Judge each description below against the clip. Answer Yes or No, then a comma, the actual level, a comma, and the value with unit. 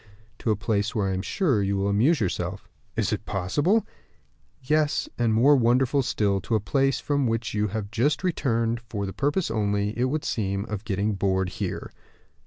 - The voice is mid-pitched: No, low, 110 Hz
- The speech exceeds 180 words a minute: Yes, average, 190 wpm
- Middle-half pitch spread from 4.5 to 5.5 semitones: Yes, average, 5.0 semitones